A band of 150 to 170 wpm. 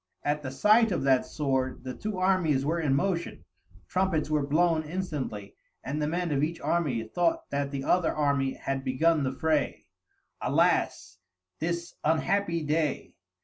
Yes: average, 155 wpm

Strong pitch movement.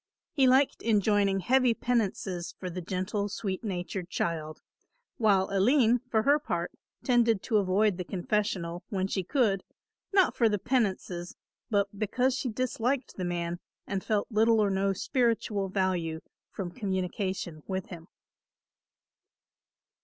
No: average, 3.7 semitones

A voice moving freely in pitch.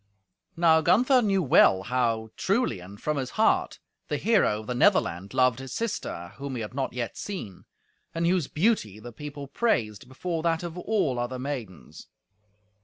Yes: wide, 7.6 semitones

